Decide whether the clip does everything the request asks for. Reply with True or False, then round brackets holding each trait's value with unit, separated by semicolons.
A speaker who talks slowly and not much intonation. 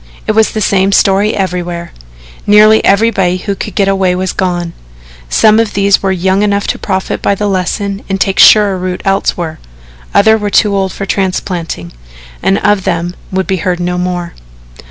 False (175 wpm; 2.0 semitones)